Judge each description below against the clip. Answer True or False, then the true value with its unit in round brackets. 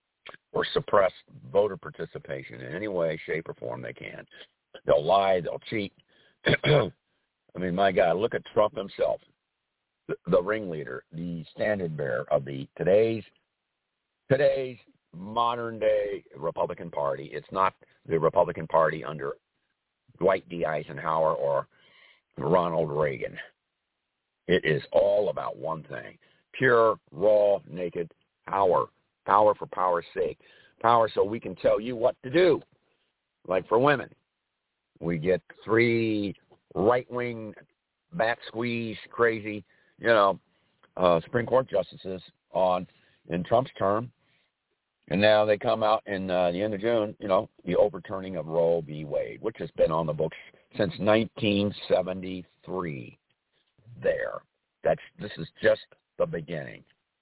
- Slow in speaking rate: True (130 wpm)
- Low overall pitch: True (110 Hz)